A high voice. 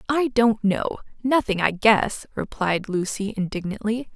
Yes: high, 215 Hz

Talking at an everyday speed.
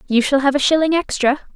No: fast, 230 wpm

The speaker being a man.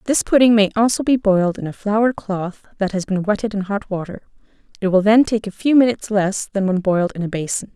No: female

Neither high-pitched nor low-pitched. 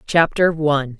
Yes: medium, 150 Hz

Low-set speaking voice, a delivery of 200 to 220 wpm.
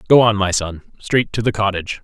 Yes: low, 105 Hz; fast, 205 wpm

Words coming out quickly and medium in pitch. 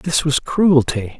No: average, 150 wpm; medium, 145 Hz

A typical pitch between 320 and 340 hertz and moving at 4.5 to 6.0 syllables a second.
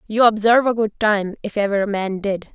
No: high, 210 Hz; 5.7 syllables/s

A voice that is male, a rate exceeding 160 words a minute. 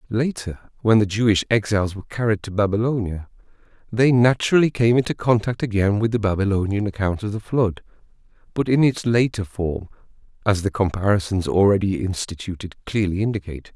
No: male; average, 150 wpm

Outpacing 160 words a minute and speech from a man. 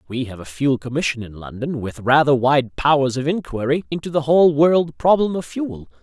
Yes: average, 200 wpm; male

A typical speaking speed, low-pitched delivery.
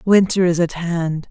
No: average, 185 wpm; medium, 175 Hz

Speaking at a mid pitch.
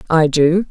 Yes: medium, 165 Hz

